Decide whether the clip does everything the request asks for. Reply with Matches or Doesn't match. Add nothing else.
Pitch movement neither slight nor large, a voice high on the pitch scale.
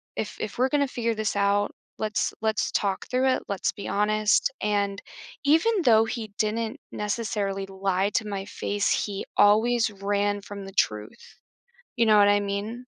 Doesn't match